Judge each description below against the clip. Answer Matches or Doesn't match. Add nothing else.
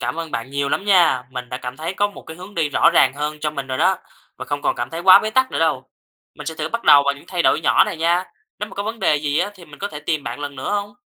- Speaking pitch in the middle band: Matches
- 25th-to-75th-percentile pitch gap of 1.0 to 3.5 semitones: Doesn't match